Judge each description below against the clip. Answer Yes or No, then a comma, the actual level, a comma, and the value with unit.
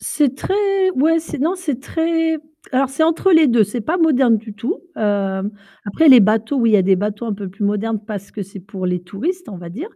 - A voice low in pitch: No, high, 230 Hz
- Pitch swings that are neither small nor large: No, wide, 7.8 semitones